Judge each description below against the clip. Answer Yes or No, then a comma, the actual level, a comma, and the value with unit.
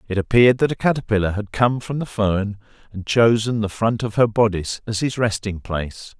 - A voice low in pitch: Yes, low, 110 Hz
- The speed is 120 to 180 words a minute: No, fast, 205 wpm